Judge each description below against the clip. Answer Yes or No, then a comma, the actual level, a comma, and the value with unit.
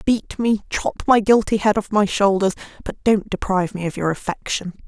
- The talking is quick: No, average, 195 wpm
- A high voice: Yes, high, 205 Hz